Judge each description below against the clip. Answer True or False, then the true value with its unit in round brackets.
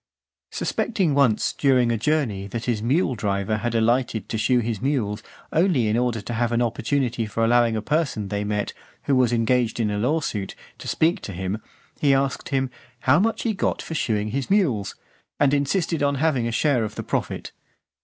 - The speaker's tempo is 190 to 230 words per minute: True (195 wpm)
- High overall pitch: False (120 Hz)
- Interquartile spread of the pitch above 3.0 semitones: True (4.5 semitones)